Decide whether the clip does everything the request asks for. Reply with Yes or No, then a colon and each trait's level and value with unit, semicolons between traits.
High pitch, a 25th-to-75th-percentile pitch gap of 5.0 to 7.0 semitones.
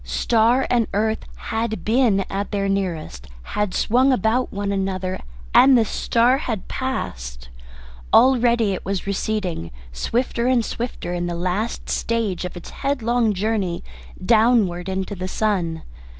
No: high, 210 Hz; average, 4.2 semitones